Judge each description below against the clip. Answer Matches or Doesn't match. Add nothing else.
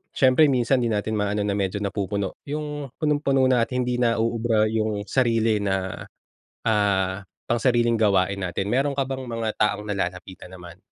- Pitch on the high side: Doesn't match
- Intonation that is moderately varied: Matches